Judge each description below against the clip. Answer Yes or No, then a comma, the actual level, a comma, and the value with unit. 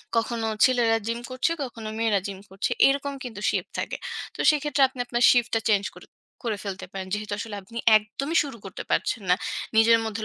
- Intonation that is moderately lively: Yes, average, 3.1 semitones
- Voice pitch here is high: Yes, high, 230 Hz